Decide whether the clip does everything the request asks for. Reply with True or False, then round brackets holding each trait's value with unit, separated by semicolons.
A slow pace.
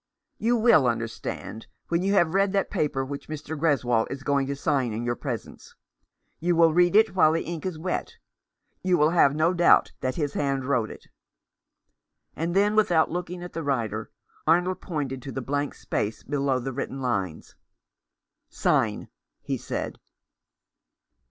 False (165 wpm)